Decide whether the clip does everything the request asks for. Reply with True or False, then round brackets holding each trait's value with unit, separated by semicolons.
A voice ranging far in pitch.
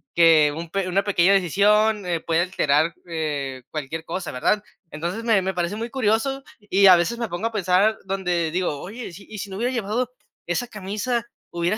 False (4.0 semitones)